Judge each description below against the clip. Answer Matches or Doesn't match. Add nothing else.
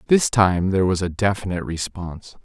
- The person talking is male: Matches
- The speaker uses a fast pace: Doesn't match